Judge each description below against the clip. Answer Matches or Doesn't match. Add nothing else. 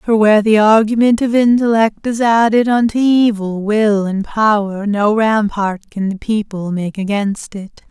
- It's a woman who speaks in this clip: Matches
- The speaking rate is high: Doesn't match